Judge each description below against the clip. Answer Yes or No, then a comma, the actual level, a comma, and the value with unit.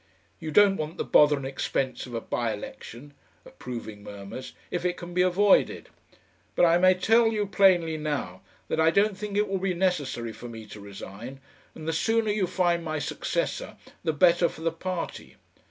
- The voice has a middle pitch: Yes, medium, 165 Hz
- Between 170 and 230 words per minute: Yes, average, 185 wpm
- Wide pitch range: Yes, wide, 6.3 semitones